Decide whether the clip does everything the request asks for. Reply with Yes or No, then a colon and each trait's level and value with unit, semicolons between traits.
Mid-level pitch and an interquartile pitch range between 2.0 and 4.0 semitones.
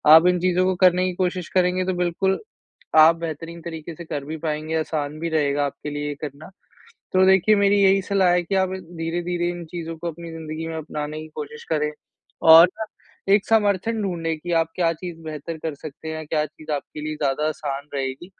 Yes: medium, 165 Hz; average, 2.8 semitones